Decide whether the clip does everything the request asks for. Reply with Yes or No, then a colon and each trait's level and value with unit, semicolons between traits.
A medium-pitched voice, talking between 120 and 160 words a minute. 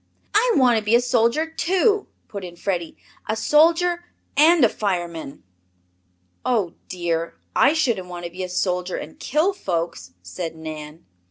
No: high, 200 Hz; average, 155 wpm